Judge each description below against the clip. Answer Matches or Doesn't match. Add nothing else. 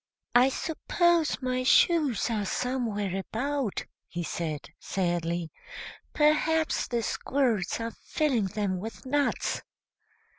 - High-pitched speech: Matches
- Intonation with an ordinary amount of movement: Doesn't match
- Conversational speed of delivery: Doesn't match